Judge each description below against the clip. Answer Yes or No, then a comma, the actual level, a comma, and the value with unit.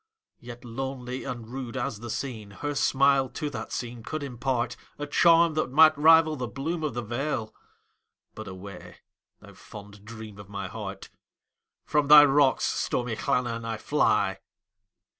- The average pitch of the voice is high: No, low, 125 Hz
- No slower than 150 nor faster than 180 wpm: No, average, 140 wpm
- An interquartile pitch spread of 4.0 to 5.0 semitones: Yes, average, 4.5 semitones